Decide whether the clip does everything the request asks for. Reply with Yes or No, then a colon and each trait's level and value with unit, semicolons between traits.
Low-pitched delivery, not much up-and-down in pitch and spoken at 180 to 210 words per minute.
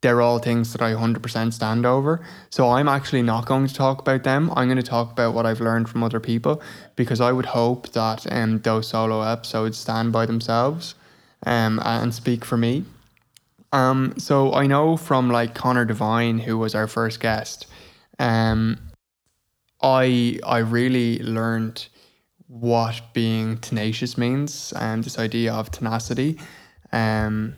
No: low, 115 Hz; narrow, 2.2 semitones; average, 160 wpm